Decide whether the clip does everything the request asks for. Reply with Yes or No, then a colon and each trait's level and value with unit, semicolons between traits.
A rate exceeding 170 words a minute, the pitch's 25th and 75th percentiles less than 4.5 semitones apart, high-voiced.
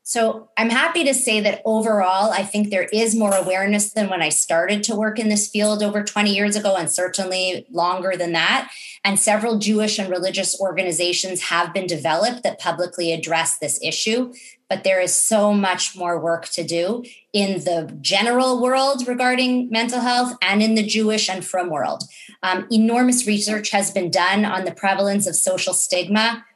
Yes: average, 180 wpm; average, 3.3 semitones; high, 200 Hz